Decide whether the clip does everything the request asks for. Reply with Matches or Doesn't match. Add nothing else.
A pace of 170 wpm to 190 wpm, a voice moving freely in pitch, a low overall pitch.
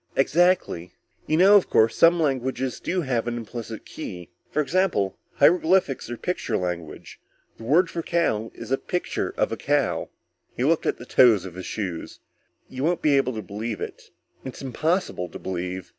Matches